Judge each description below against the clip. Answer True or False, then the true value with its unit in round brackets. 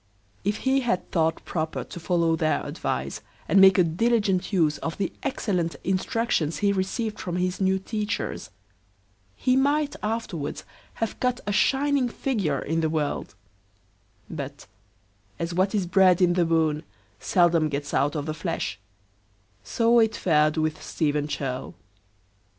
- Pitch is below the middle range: False (180 Hz)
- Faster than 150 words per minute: False (145 wpm)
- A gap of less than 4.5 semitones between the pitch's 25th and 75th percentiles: False (5.2 semitones)